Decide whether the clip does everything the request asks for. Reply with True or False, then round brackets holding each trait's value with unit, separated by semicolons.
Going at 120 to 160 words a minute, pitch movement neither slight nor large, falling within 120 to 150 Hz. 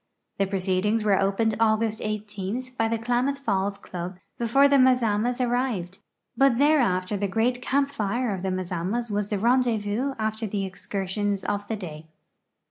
False (155 wpm; 3.9 semitones; 215 Hz)